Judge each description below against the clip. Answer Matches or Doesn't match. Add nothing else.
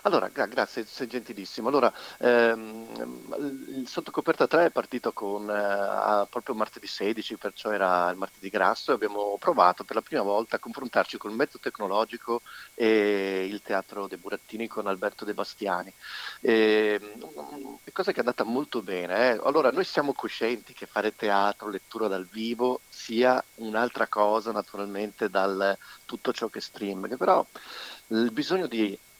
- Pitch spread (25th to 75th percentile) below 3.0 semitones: Matches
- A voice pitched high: Doesn't match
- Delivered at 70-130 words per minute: Doesn't match